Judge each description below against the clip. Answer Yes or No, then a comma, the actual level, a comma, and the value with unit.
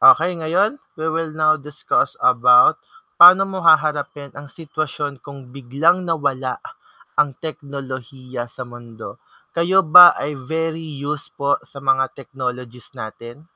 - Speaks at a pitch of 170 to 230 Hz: No, medium, 145 Hz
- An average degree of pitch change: Yes, average, 3.8 semitones